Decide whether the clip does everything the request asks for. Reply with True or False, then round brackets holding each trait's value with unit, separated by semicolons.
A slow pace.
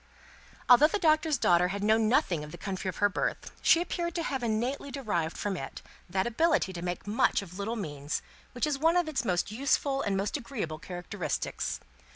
False (200 wpm)